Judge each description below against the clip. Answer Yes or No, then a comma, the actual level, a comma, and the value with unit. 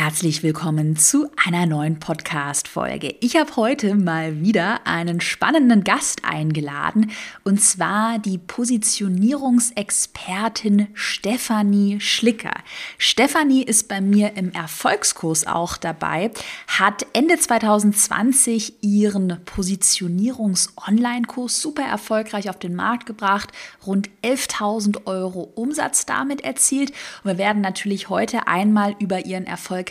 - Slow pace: Yes, slow, 110 wpm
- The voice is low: No, high, 205 Hz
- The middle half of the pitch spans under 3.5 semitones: No, average, 4.0 semitones